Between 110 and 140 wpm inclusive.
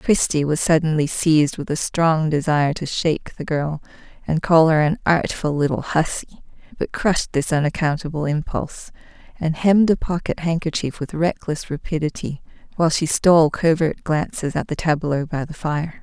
No: average, 160 wpm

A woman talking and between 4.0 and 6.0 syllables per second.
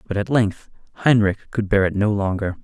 No: male; 5.5 syllables/s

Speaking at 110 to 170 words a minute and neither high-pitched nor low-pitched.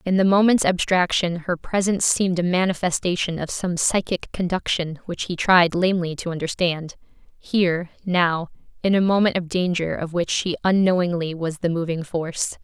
Yes: average, 155 wpm; medium, 175 Hz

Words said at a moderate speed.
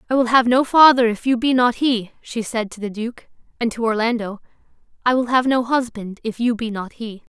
No: fast, 230 wpm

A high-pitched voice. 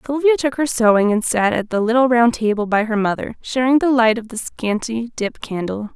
Yes: high, 230 Hz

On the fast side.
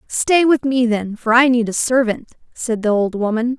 Yes: fast, 215 wpm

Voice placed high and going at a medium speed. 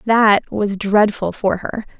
Yes: high, 205 Hz; average, 150 wpm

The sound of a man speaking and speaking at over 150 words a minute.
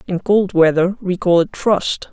No: female; average, 200 wpm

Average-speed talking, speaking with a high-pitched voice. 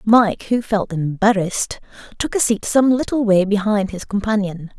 Yes: average, 165 wpm; high, 210 Hz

